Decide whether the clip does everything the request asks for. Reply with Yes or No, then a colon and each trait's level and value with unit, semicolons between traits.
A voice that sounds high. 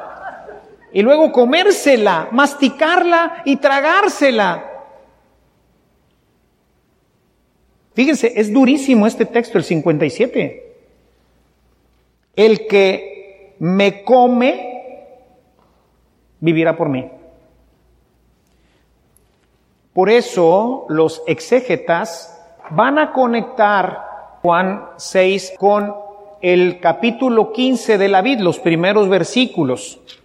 Yes: high, 210 Hz